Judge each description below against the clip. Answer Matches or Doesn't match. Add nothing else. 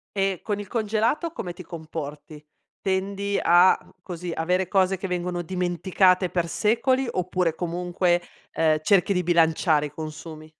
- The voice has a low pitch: Doesn't match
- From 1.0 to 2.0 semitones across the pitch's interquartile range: Doesn't match